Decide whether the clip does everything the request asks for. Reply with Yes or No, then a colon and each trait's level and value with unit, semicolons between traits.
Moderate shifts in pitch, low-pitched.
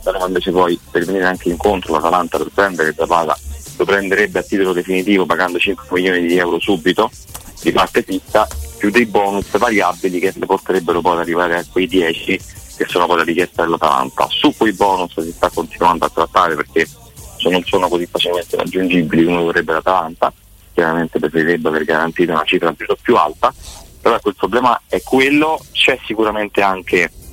No: narrow, 2.0 semitones; very low, 90 Hz